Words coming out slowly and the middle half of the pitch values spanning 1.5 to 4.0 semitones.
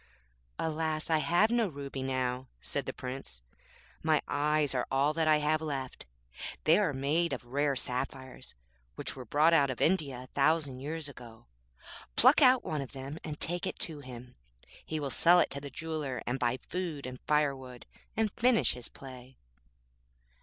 No: average, 175 wpm; average, 3.4 semitones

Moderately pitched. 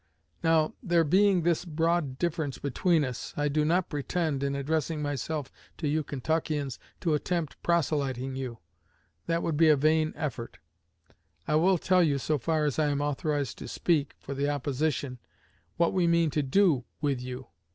Yes: medium, 150 Hz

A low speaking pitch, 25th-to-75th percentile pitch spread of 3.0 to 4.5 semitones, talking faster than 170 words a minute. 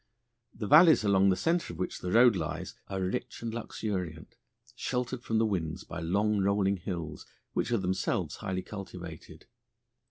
No: low, 100 Hz; average, 3.7 semitones; average, 160 wpm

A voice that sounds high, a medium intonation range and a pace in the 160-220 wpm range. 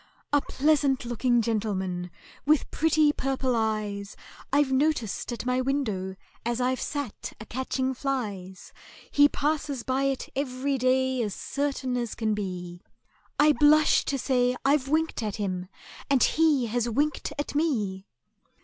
No: very high, 255 Hz; average, 4.7 semitones; average, 140 wpm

